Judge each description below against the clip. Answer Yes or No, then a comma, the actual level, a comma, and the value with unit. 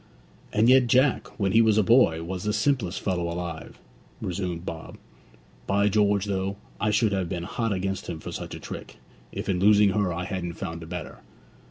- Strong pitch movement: No, average, 3.2 semitones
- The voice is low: Yes, very low, 95 Hz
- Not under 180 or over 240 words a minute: Yes, average, 195 wpm